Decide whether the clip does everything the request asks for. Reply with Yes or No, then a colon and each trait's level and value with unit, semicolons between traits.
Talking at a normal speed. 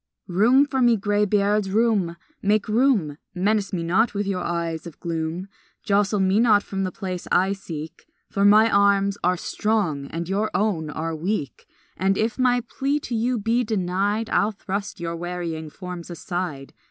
Yes: average, 165 wpm